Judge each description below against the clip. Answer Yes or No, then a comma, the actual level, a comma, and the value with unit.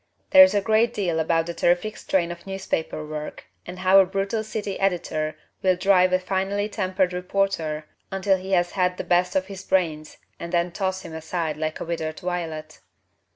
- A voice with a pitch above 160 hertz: Yes, medium, 185 Hz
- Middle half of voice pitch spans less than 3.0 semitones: Yes, narrow, 2.5 semitones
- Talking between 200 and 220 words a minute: No, average, 190 wpm